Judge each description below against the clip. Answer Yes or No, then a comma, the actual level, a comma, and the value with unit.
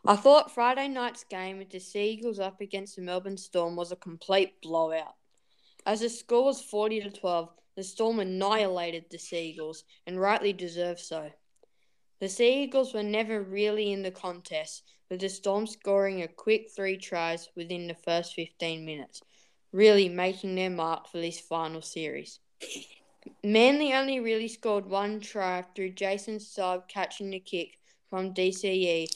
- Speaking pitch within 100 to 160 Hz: No, high, 190 Hz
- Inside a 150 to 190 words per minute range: Yes, fast, 155 wpm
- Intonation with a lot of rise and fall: No, average, 3.5 semitones